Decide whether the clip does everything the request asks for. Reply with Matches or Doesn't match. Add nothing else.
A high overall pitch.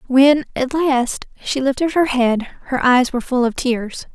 Matches